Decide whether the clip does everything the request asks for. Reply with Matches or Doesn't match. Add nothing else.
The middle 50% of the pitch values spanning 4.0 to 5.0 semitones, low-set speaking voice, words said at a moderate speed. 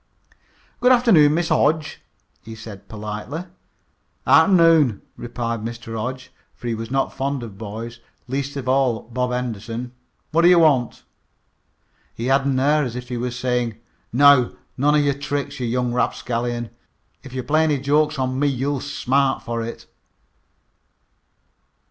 Doesn't match